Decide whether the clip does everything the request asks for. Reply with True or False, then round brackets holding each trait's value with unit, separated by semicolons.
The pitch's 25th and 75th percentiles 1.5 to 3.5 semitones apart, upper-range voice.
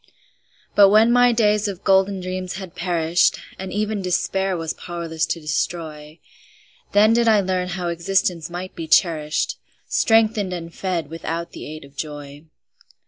False (3.2 semitones; 180 Hz)